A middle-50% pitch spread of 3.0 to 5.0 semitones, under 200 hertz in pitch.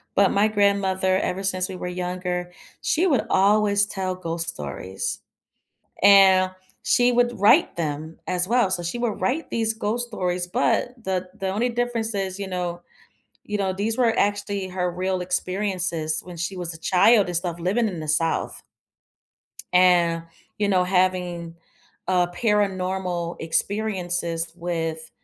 No: narrow, 2.5 semitones; medium, 185 Hz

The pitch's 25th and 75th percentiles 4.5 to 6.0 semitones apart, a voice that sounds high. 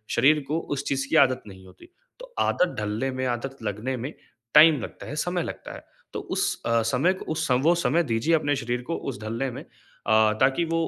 No: wide, 5.4 semitones; low, 135 Hz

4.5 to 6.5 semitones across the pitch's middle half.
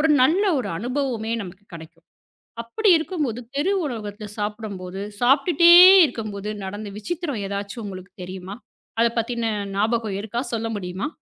No: average, 4.1 semitones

